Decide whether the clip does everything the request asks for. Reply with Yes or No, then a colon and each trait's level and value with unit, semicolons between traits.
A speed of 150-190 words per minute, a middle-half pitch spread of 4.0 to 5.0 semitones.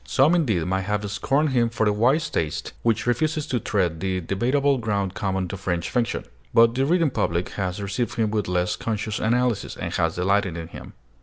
No: average, 200 wpm; average, 4.7 semitones